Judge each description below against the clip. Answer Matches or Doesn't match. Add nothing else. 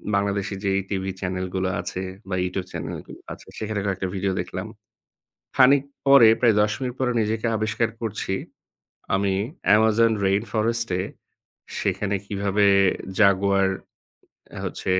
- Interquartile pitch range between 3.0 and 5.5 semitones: Doesn't match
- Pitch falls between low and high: Doesn't match